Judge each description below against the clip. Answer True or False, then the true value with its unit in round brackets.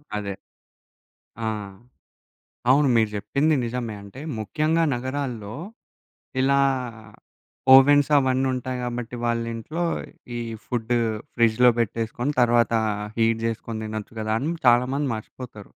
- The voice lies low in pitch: True (120 Hz)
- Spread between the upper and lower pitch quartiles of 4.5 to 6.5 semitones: False (3.0 semitones)